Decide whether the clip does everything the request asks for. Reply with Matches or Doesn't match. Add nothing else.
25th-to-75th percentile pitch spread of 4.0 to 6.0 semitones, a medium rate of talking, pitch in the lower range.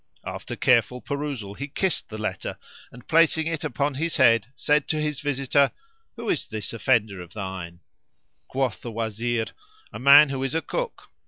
Matches